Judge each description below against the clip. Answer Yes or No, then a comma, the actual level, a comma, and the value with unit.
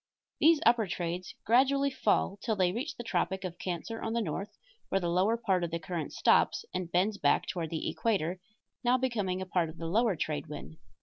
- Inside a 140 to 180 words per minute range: No, fast, 205 wpm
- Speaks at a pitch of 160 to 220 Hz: Yes, high, 190 Hz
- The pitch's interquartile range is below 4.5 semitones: No, average, 4.8 semitones